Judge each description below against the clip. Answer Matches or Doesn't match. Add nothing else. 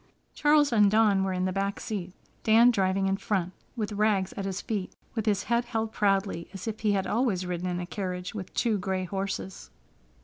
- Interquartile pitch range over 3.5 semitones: Doesn't match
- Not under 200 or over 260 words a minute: Matches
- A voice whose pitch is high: Matches